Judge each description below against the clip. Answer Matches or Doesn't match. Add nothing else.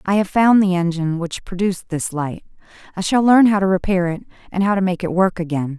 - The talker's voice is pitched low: Doesn't match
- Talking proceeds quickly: Matches